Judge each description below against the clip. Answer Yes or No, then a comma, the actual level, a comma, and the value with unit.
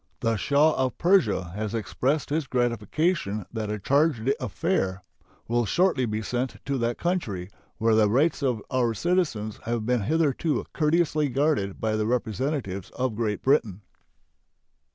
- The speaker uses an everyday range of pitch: No, wide, 5.8 semitones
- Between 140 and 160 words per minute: Yes, average, 145 wpm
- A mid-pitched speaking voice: No, low, 120 Hz